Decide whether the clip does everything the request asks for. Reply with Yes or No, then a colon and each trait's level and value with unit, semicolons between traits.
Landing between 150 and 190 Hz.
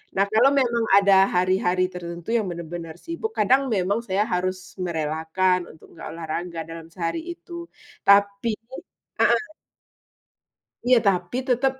Yes: medium, 185 Hz